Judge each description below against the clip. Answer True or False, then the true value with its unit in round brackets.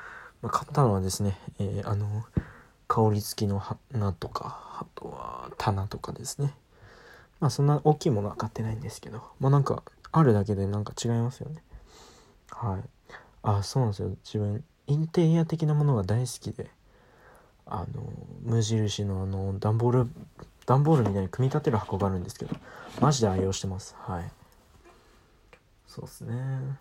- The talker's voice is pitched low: True (115 Hz)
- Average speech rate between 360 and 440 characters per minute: False (325 characters per minute)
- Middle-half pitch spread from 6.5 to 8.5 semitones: False (5.6 semitones)